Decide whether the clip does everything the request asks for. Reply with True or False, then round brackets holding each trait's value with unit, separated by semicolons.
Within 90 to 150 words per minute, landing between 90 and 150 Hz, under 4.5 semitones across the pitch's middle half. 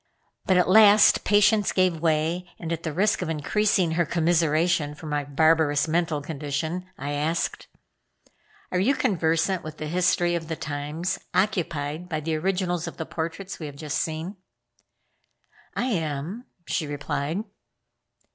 False (145 wpm; 165 Hz; 2.9 semitones)